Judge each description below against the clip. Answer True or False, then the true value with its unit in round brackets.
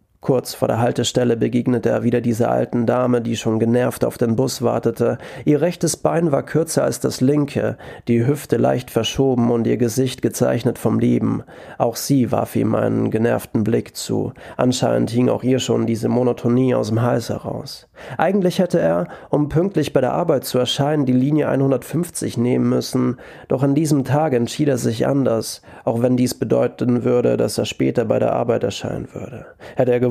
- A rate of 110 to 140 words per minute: False (185 wpm)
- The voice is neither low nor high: False (125 Hz)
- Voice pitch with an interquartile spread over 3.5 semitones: False (2.9 semitones)